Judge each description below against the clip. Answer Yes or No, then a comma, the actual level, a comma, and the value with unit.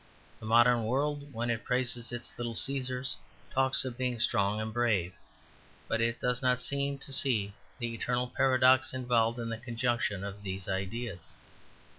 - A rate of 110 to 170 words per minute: Yes, average, 160 wpm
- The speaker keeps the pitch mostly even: Yes, narrow, 2.3 semitones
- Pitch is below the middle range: Yes, low, 120 Hz